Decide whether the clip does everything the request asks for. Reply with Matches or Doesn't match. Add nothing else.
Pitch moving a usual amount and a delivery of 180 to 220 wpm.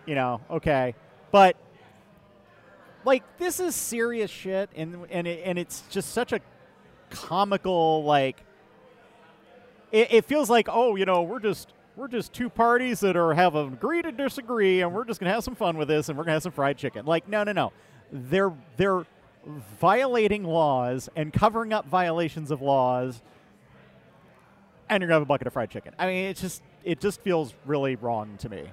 Doesn't match